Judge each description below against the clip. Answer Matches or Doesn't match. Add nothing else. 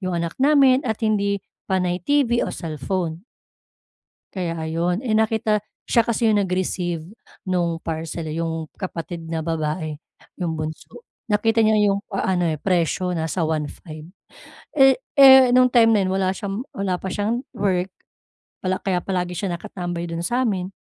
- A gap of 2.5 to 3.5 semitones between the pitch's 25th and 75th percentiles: Doesn't match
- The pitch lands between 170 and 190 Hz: Matches